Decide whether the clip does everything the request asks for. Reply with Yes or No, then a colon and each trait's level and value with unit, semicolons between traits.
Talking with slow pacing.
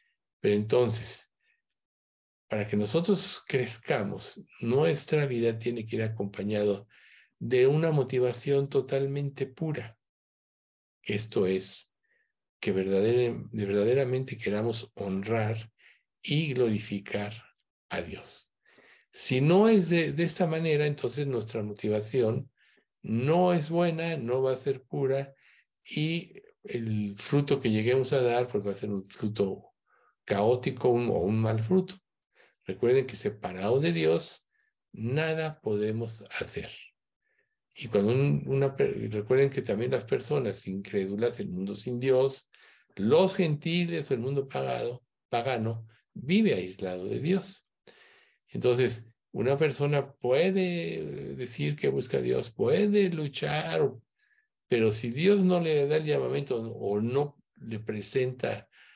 Yes: slow, 120 wpm